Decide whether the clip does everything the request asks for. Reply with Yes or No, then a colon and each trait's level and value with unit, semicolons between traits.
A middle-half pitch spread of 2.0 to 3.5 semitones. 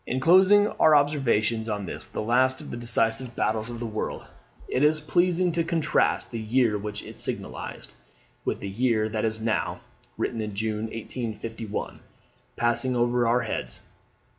Yes: average, 3.0 semitones